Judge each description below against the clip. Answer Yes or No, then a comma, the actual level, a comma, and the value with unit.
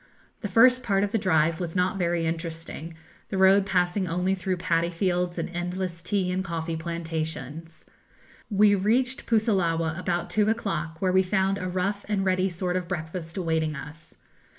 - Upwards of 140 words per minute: Yes, average, 170 wpm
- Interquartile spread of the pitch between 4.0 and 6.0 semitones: No, average, 2.7 semitones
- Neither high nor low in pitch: Yes, medium, 180 Hz